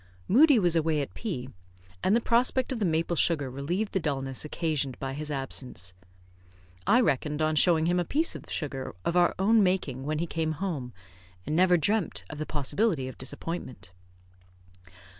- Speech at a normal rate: Yes, average, 175 wpm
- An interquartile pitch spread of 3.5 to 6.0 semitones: Yes, average, 5.2 semitones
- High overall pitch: No, medium, 160 Hz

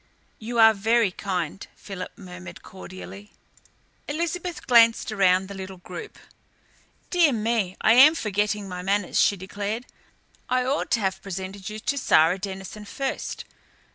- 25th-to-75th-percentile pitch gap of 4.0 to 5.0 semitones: No, average, 3.6 semitones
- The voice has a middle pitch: No, high, 205 Hz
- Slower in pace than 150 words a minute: Yes, average, 140 wpm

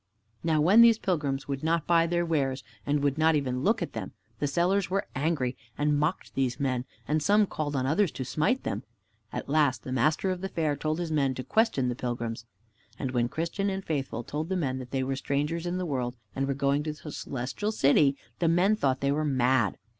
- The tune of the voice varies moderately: Yes, average, 4.2 semitones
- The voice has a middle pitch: Yes, medium, 150 Hz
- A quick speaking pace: Yes, fast, 220 wpm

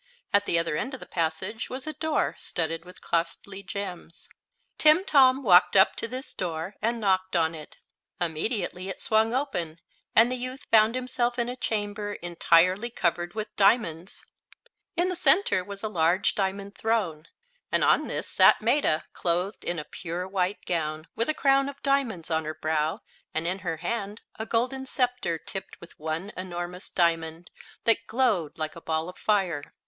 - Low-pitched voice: No, high, 190 Hz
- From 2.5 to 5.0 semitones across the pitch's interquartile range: No, wide, 5.6 semitones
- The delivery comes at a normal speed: Yes, average, 175 wpm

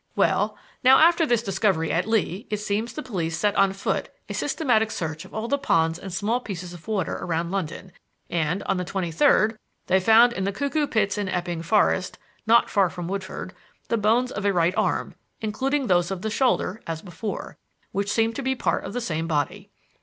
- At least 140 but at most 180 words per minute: No, fast, 205 wpm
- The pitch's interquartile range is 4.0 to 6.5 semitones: Yes, average, 4.3 semitones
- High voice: Yes, high, 200 Hz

